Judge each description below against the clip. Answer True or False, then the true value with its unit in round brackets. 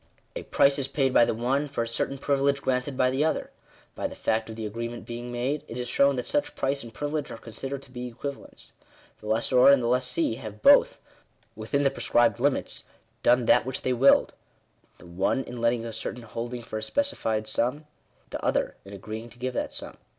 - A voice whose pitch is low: True (125 Hz)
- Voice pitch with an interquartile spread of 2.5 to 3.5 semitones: True (3.0 semitones)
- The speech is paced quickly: True (215 wpm)